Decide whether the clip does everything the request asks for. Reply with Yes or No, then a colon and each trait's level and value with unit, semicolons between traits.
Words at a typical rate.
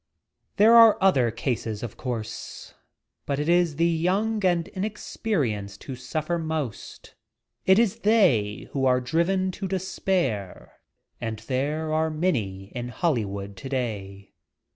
No: slow, 125 wpm